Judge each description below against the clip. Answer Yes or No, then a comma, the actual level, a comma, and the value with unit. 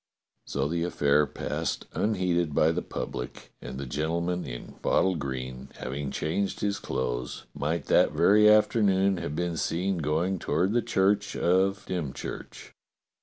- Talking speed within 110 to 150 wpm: Yes, average, 140 wpm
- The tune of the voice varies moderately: Yes, average, 5.0 semitones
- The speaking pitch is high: No, very low, 85 Hz